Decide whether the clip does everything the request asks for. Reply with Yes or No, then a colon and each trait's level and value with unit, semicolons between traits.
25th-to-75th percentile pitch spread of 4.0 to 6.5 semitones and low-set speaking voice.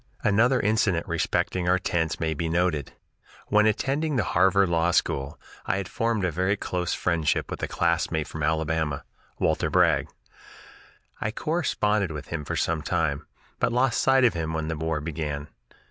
Yes: average, 4.7 semitones; very low, 85 Hz